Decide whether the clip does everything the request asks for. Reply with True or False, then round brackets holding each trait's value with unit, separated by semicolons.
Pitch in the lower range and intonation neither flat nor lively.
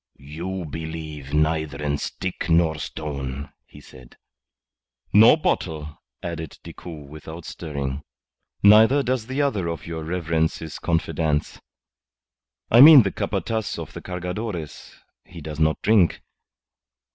True (80 Hz; 3.7 semitones)